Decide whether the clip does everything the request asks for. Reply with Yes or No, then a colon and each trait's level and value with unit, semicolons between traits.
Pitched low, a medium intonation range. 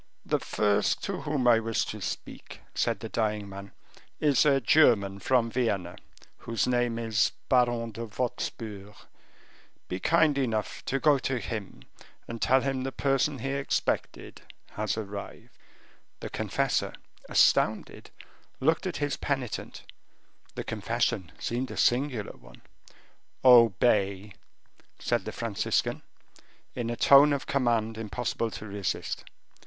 Yes: low, 115 Hz; average, 4.2 semitones